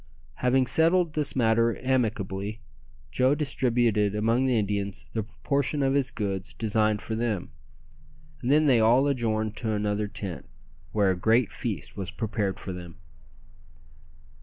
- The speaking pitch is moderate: No, low, 110 Hz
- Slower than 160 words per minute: Yes, average, 140 wpm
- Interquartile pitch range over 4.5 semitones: No, average, 3.9 semitones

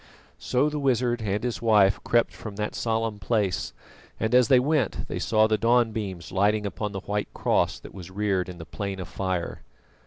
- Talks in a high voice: No, low, 105 Hz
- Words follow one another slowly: No, average, 195 wpm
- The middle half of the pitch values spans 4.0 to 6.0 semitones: No, average, 3.3 semitones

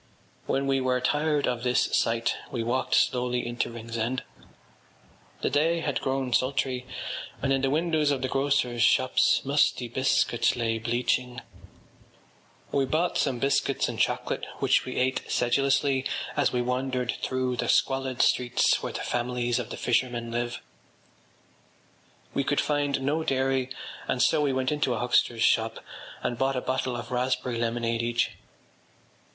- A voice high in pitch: No, low, 130 Hz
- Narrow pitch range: Yes, narrow, 2.1 semitones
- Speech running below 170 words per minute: Yes, average, 155 wpm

